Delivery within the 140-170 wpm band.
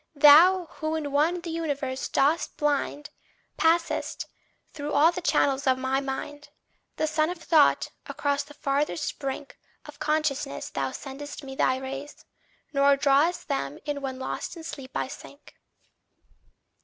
Yes: average, 145 wpm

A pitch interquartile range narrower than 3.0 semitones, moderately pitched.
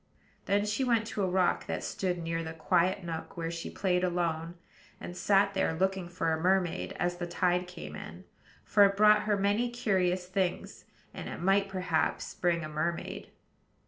Yes: narrow, 2.5 semitones; medium, 180 Hz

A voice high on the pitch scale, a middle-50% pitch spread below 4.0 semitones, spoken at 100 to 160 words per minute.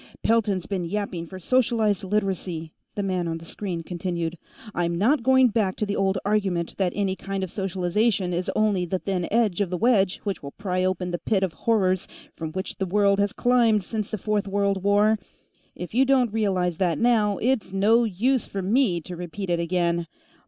No: high, 195 Hz; average, 3.0 semitones; average, 195 wpm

